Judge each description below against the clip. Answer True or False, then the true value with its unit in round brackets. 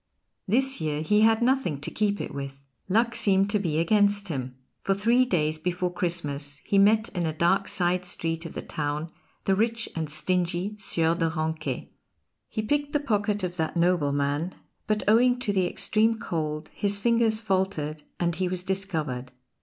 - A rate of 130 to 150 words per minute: False (175 wpm)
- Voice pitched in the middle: True (180 Hz)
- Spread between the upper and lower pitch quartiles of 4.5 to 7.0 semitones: True (5.0 semitones)